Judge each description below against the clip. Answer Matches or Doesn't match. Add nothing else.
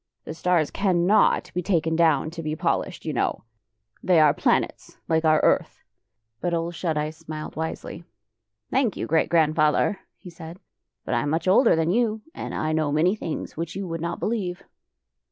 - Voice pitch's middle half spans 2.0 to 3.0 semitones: Matches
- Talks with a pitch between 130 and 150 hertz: Doesn't match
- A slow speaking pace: Doesn't match